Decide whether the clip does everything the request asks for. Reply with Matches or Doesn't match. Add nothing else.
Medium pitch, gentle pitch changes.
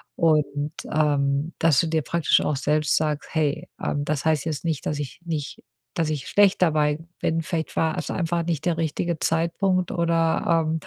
Matches